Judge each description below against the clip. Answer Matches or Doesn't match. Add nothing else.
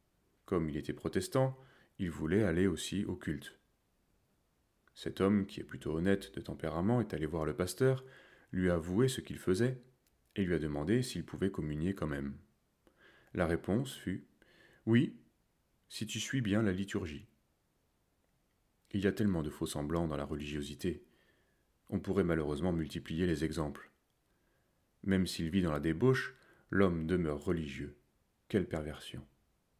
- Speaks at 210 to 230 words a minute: Doesn't match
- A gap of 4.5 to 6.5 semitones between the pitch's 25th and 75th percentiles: Matches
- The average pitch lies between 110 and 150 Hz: Doesn't match